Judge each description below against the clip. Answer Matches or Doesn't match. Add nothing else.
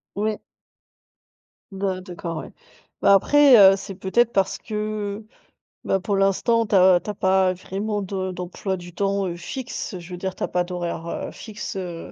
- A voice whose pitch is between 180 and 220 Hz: Matches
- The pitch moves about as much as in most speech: Doesn't match